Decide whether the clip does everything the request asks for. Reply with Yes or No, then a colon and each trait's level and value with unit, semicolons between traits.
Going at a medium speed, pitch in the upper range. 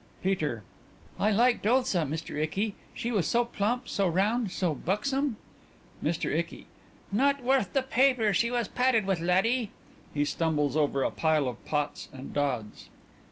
Yes: average, 160 wpm; high, 195 Hz